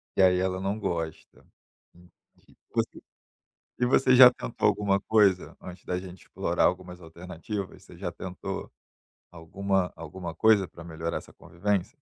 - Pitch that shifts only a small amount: Yes, narrow, 2.3 semitones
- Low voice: Yes, very low, 90 Hz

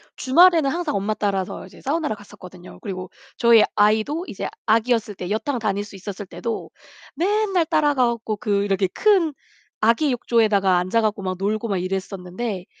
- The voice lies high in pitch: Yes, high, 215 Hz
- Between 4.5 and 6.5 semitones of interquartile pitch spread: Yes, wide, 5.4 semitones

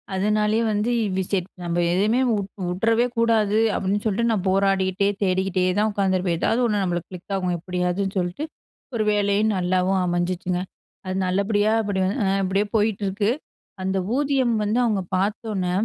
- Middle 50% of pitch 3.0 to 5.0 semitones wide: No, narrow, 2.5 semitones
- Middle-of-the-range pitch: No, high, 195 Hz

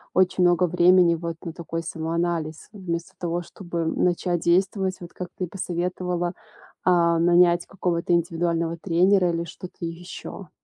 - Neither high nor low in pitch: Yes, medium, 175 Hz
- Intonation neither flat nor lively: No, narrow, 1.2 semitones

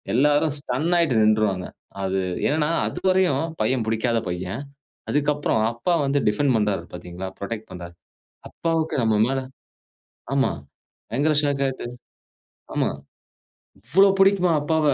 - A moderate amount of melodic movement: No, wide, 5.9 semitones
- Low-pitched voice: Yes, low, 130 Hz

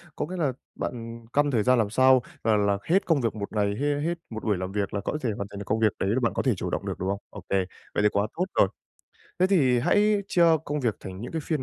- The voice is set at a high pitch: No, low, 115 Hz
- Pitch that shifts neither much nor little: No, wide, 6.2 semitones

